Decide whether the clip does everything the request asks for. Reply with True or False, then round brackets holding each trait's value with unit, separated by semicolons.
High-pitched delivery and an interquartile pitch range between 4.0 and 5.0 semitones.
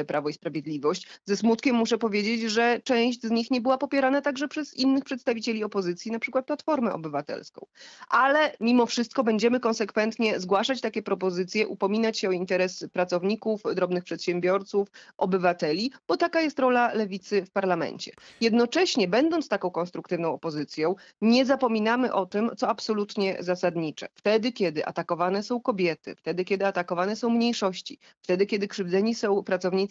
True (215 Hz; 4.7 semitones)